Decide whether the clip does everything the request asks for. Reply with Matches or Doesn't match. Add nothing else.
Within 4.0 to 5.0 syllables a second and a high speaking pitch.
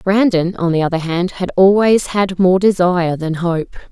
Doesn't match